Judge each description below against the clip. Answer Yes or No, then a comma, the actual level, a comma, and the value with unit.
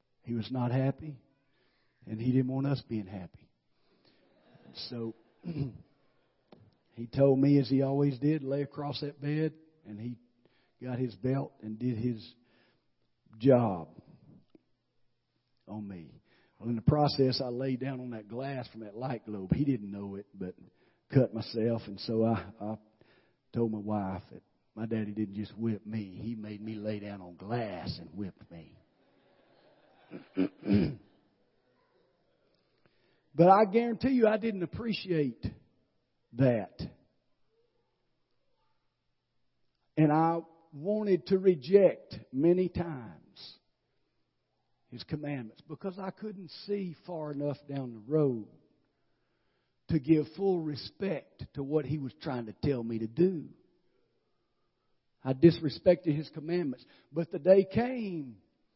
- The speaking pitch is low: Yes, low, 130 Hz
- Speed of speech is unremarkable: No, slow, 130 wpm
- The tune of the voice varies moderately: No, wide, 5.7 semitones